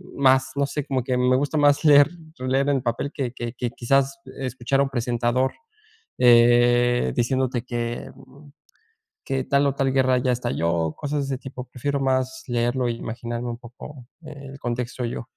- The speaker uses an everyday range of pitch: No, narrow, 2.2 semitones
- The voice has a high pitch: No, low, 130 Hz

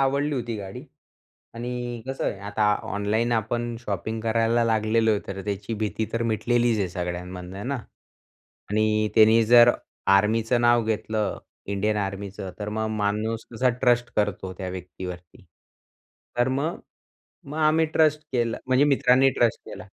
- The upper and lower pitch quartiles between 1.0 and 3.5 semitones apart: Yes, average, 2.8 semitones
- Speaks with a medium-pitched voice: No, low, 110 Hz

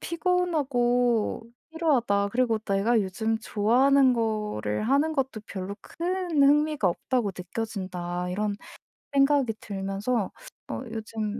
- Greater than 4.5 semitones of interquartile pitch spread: Yes, wide, 5.4 semitones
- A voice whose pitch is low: No, high, 225 Hz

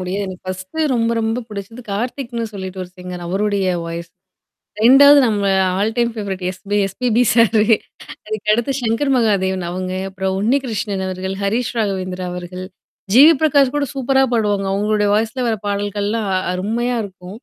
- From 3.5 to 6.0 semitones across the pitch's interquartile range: Yes, average, 3.8 semitones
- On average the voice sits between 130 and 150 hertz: No, high, 210 Hz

